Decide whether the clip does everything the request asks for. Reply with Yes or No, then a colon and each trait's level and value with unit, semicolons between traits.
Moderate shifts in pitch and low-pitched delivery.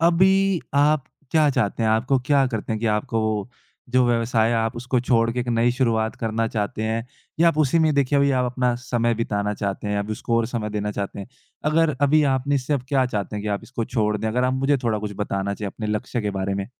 Yes: average, 3.8 semitones; low, 115 Hz